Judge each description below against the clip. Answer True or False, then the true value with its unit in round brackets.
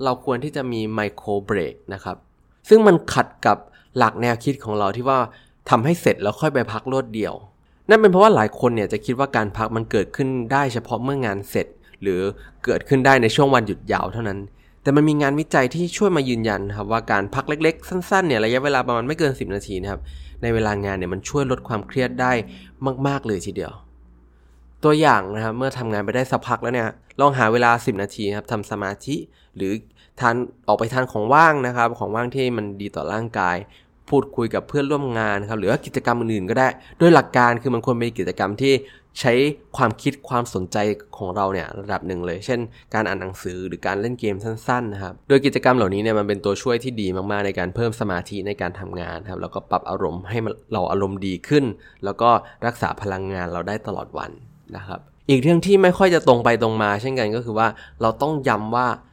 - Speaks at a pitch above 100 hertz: True (115 Hz)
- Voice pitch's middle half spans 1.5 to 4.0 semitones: False (4.7 semitones)